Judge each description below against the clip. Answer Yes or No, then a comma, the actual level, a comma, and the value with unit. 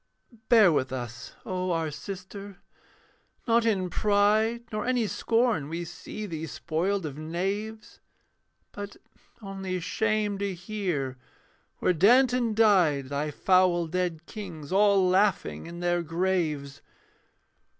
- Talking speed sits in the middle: No, slow, 120 wpm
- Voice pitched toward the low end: No, medium, 185 Hz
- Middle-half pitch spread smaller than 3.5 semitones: No, average, 4.3 semitones